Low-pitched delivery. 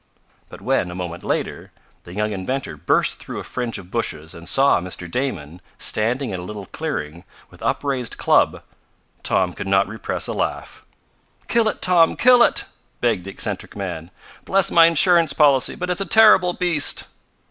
Yes: low, 115 Hz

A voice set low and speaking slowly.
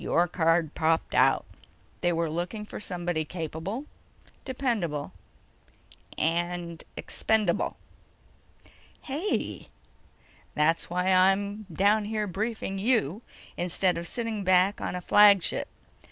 No: medium, 185 Hz; slow, 105 wpm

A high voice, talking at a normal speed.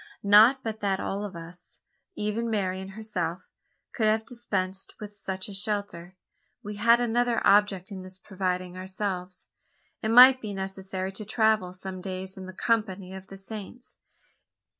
Yes: high, 195 Hz; average, 155 wpm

